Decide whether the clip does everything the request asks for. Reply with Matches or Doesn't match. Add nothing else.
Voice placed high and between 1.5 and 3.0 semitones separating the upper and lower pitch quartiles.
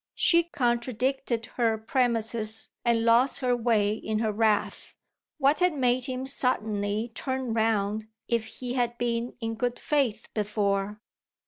Matches